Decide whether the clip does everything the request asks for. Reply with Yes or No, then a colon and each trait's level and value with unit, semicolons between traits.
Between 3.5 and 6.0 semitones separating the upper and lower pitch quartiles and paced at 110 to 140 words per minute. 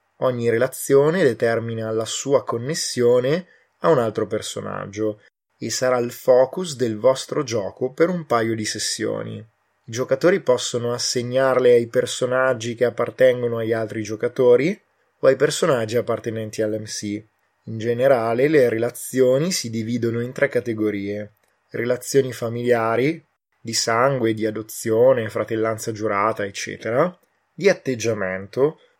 No: narrow, 2.5 semitones; average, 120 wpm